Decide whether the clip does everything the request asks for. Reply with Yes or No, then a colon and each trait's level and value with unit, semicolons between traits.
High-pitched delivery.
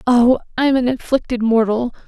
Yes: high, 240 Hz